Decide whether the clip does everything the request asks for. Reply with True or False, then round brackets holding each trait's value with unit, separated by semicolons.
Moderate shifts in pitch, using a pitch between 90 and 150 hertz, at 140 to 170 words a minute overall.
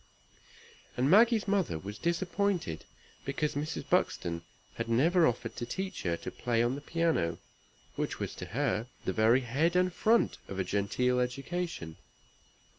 False (8.0 semitones; 135 Hz; 150 wpm)